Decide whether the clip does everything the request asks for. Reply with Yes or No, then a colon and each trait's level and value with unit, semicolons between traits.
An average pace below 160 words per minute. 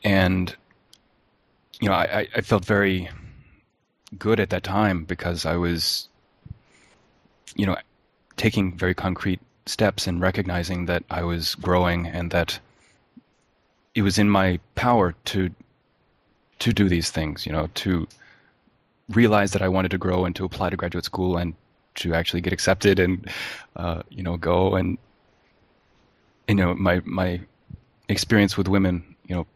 Yes: average, 150 wpm